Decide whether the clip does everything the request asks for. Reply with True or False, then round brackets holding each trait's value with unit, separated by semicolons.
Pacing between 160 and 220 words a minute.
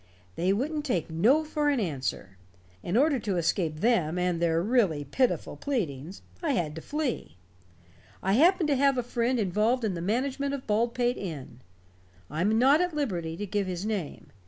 True (180 wpm)